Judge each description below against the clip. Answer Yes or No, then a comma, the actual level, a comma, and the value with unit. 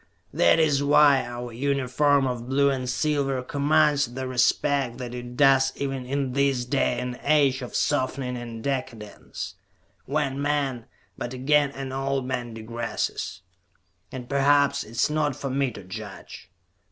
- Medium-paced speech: Yes, average, 150 wpm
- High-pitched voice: No, low, 135 Hz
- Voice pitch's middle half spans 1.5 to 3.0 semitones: Yes, narrow, 2.4 semitones